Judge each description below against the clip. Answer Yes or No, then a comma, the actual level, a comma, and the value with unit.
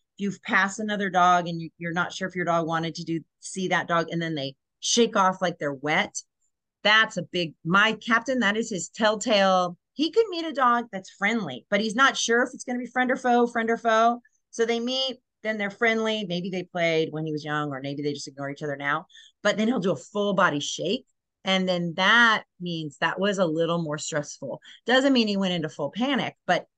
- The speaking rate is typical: No, fast, 235 wpm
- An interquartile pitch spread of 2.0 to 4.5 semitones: No, wide, 5.5 semitones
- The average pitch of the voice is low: No, high, 190 Hz